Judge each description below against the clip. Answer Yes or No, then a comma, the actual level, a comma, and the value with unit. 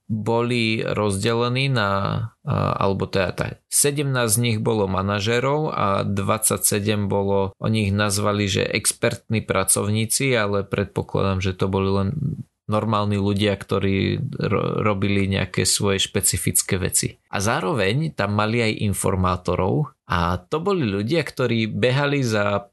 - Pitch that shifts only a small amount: No, average, 3.4 semitones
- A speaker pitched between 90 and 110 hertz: Yes, low, 105 Hz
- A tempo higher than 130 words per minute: No, average, 125 wpm